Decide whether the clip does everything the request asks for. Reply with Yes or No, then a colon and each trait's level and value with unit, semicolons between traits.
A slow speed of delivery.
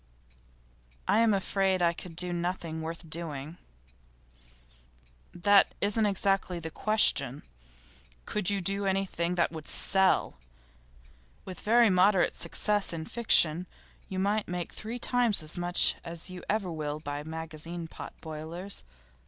Yes: slow, 130 wpm